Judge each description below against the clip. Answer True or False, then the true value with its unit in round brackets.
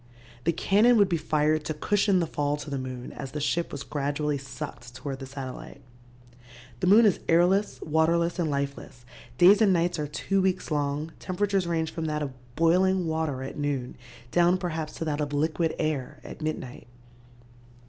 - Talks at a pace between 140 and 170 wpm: False (180 wpm)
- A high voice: False (155 Hz)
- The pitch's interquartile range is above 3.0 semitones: True (3.5 semitones)